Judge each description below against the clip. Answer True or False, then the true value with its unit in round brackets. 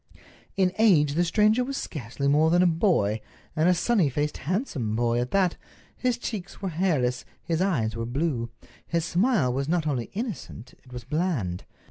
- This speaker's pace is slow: False (175 wpm)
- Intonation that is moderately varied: False (6.9 semitones)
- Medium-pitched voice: True (160 Hz)